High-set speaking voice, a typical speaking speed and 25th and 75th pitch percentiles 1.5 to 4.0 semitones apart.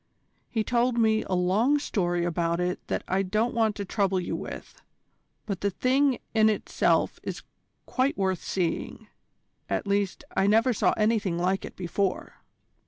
Yes: high, 200 Hz; average, 160 wpm; average, 3.6 semitones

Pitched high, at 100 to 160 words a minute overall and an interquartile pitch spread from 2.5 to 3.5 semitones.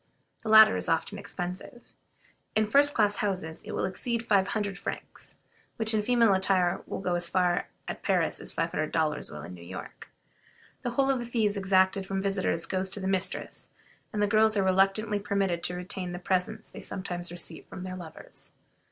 No: high, 195 Hz; average, 195 wpm; average, 3.2 semitones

